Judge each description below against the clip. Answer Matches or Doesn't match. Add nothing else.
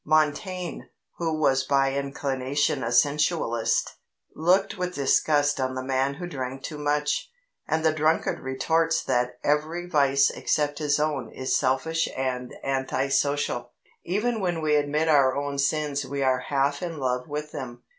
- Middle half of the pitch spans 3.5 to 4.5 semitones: Doesn't match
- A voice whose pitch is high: Doesn't match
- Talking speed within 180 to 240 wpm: Doesn't match